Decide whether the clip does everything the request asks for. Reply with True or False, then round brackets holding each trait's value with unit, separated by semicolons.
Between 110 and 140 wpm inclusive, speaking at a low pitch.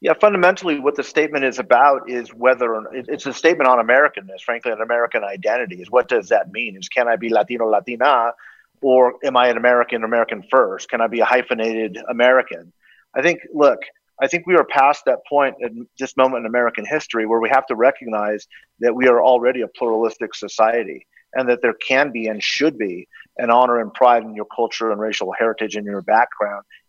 False (205 wpm; 120 Hz)